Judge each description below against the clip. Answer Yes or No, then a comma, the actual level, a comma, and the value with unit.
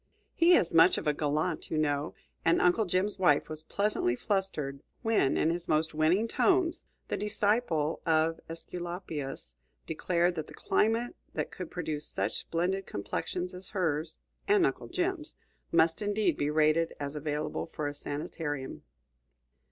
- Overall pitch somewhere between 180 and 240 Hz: No, medium, 165 Hz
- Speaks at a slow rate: No, average, 150 wpm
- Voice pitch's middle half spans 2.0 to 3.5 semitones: No, average, 4.2 semitones